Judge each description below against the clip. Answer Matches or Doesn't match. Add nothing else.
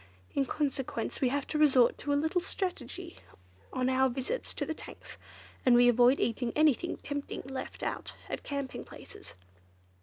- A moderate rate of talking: Matches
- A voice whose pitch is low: Doesn't match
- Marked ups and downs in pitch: Doesn't match